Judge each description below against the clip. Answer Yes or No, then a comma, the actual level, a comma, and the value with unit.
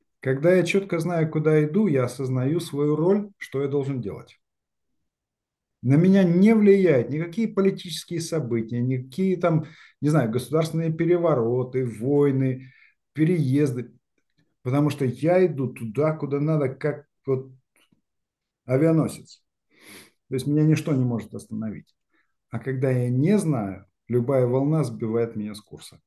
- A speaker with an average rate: Yes, average, 130 wpm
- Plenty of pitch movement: No, average, 4.3 semitones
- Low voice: No, medium, 145 Hz